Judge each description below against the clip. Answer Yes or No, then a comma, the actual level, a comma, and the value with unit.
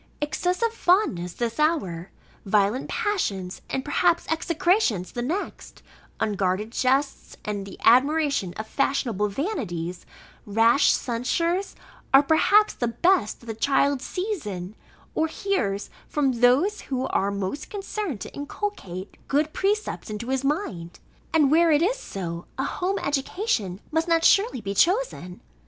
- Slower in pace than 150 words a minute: Yes, slow, 135 wpm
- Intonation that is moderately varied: No, wide, 8.7 semitones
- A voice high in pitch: Yes, very high, 275 Hz